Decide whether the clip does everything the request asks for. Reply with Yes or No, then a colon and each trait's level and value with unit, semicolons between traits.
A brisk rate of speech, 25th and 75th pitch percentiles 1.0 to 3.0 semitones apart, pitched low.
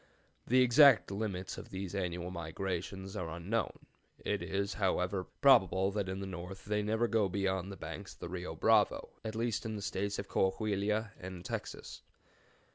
No: average, 170 wpm; narrow, 2.4 semitones; very low, 95 Hz